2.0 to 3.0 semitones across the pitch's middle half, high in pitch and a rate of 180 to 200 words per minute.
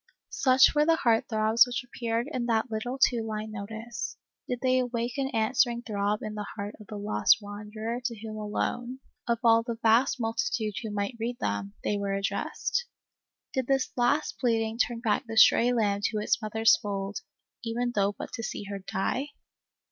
Yes: narrow, 2.5 semitones; high, 225 Hz; average, 185 wpm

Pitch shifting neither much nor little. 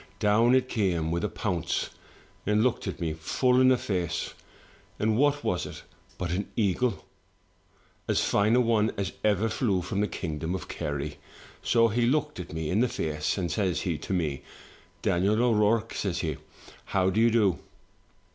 Yes: average, 4.8 semitones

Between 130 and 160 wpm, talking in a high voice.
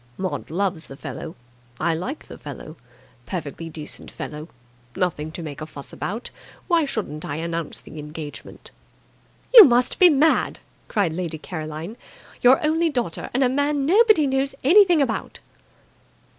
Yes: average, 145 wpm; high, 195 Hz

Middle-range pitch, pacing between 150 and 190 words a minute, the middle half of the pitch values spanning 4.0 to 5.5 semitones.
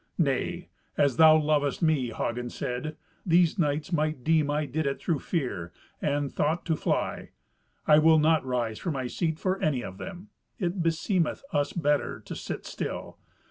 No: medium, 155 Hz; average, 170 wpm; average, 3.0 semitones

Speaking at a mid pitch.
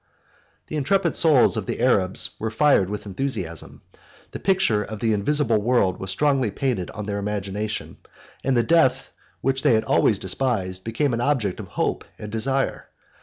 No: low, 110 Hz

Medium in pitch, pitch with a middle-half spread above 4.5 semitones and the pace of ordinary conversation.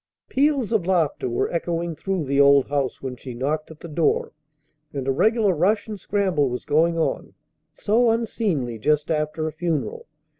Yes: medium, 160 Hz; wide, 5.6 semitones; average, 175 wpm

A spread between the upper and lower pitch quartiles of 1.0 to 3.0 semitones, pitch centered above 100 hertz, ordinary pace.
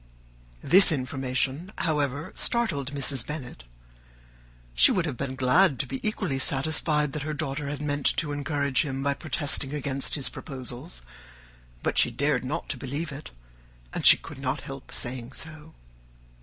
Yes: narrow, 2.4 semitones; medium, 140 Hz; average, 145 wpm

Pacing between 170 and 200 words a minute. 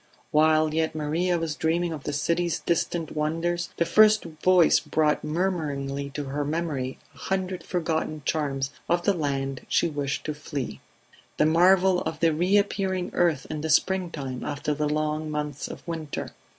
No: average, 160 wpm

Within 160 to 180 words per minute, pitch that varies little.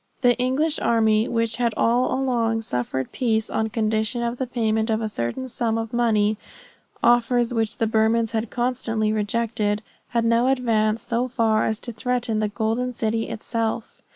Yes: average, 165 wpm; narrow, 1.8 semitones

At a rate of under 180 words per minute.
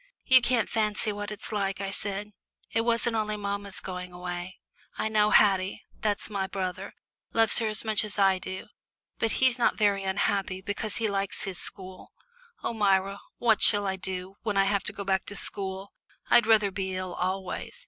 No: average, 190 wpm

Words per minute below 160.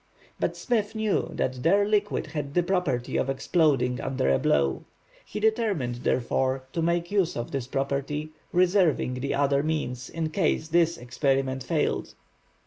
Yes: average, 150 wpm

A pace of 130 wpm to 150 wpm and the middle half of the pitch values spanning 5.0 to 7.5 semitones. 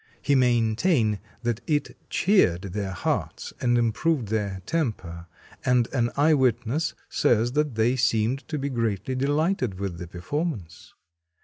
Yes: slow, 135 wpm; average, 5.3 semitones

